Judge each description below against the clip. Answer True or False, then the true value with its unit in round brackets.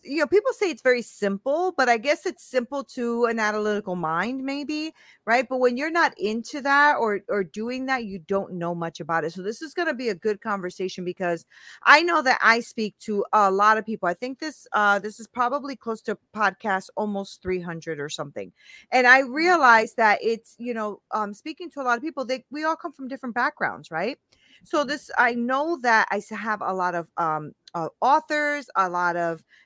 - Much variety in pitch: True (5.7 semitones)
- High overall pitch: True (230 Hz)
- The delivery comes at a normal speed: False (215 wpm)